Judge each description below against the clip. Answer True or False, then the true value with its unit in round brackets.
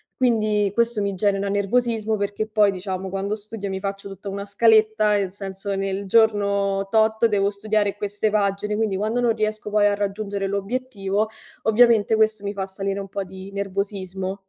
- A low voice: False (205 Hz)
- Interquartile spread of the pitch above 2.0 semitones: False (1.7 semitones)